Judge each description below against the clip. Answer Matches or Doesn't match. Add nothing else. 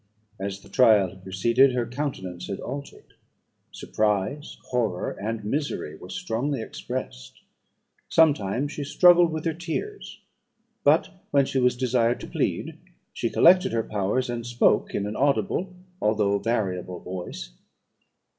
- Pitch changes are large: Matches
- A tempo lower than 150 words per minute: Matches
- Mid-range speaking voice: Doesn't match